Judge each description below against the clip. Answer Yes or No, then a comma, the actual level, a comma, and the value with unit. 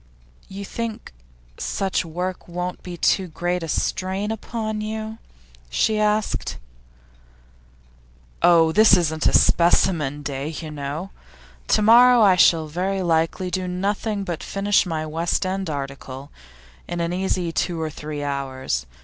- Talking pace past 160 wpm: No, slow, 135 wpm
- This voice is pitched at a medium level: Yes, medium, 180 Hz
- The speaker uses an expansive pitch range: No, average, 3.9 semitones